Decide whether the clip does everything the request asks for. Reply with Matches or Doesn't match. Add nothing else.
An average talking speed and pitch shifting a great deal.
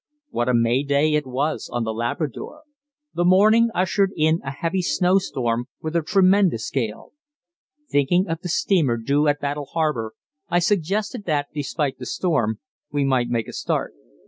Matches